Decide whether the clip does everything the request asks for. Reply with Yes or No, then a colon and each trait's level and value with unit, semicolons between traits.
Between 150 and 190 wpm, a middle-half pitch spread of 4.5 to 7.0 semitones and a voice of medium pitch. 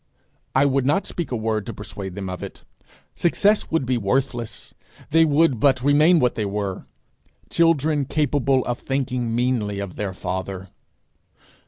No: average, 155 wpm; wide, 5.6 semitones; low, 125 Hz